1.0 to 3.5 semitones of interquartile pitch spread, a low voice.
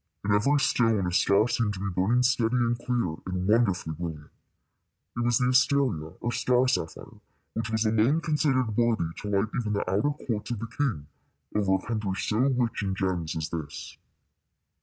No: average, 4.5 semitones; low, 110 Hz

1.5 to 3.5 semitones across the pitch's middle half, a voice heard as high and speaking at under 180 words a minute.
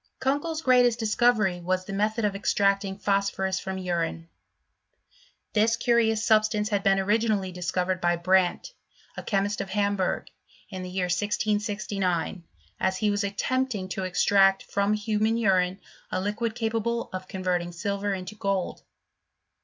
Yes: narrow, 2.6 semitones; high, 200 Hz; slow, 135 wpm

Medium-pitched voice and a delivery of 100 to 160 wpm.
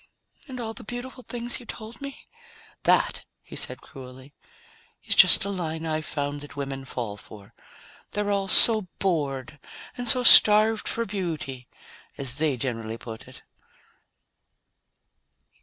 Yes: medium, 160 Hz; average, 140 wpm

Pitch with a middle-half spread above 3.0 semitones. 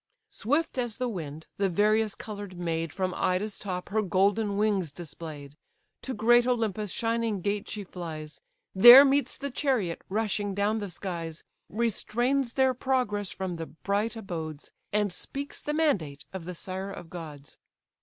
Yes: average, 4.6 semitones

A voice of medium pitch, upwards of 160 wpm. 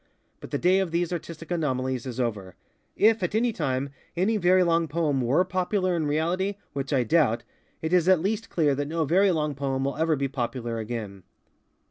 Yes: medium, 160 Hz; average, 195 wpm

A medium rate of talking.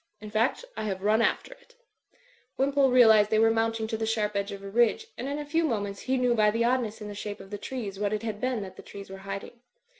No: fast, 265 wpm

